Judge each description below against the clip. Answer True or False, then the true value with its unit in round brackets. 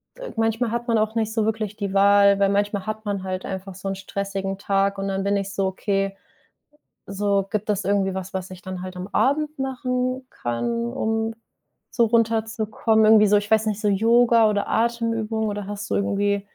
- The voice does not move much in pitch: True (2.3 semitones)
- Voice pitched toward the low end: False (205 Hz)